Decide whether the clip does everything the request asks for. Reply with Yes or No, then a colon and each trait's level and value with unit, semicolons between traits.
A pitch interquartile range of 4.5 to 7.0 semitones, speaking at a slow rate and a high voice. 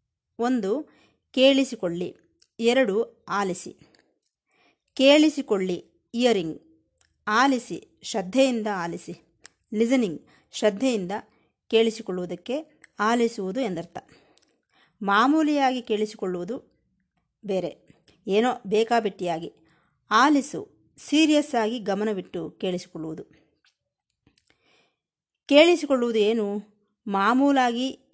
Yes: average, 5.2 semitones; slow, 55 wpm; high, 215 Hz